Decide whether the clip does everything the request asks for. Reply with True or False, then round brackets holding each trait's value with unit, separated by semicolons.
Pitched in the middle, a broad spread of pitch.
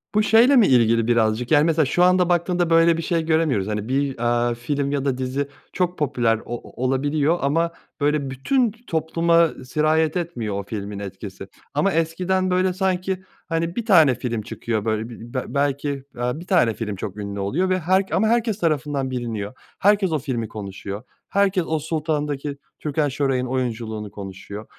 True (145 Hz; 6.2 semitones)